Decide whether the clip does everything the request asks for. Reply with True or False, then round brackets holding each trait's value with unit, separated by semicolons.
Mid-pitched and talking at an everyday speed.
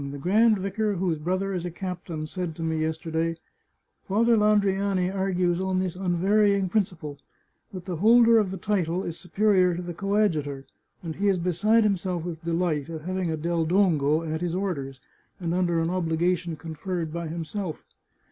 True (180 Hz; 175 wpm)